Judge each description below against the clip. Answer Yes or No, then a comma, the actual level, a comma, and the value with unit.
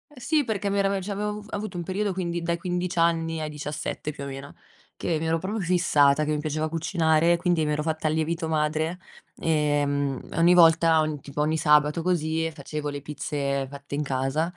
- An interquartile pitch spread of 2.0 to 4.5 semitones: Yes, narrow, 2.5 semitones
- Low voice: No, medium, 160 Hz